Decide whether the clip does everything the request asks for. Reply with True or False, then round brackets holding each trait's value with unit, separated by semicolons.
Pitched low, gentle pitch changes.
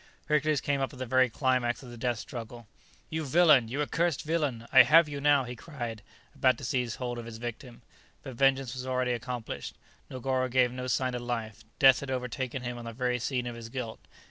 True (125 Hz; 2.1 semitones)